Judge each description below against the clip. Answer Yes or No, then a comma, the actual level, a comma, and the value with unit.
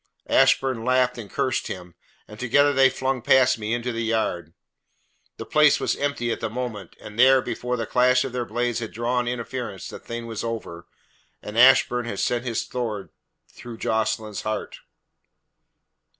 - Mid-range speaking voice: No, low, 120 Hz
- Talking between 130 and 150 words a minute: No, average, 165 wpm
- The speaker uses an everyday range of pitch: No, narrow, 2.3 semitones